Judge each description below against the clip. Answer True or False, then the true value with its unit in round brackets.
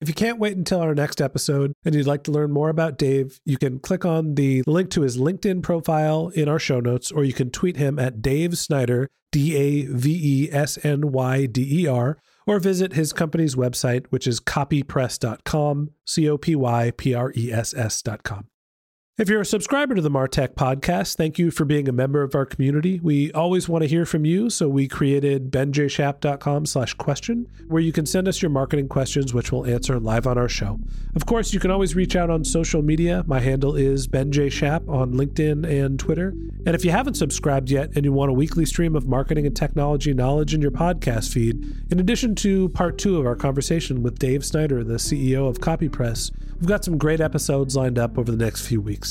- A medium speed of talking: False (215 wpm)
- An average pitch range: True (3.7 semitones)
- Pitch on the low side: False (145 Hz)